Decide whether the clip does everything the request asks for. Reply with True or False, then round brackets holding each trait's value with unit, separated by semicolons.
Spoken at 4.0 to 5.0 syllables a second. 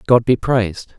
False (5.4 syllables/s)